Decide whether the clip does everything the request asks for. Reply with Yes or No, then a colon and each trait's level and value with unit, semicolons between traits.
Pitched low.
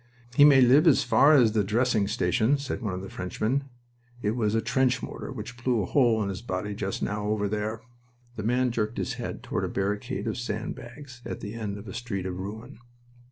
Yes: low, 110 Hz